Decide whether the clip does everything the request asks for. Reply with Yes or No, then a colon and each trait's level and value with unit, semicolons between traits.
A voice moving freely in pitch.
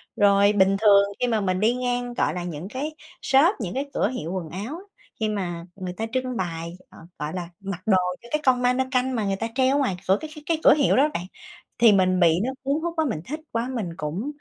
Yes: wide, 5.9 semitones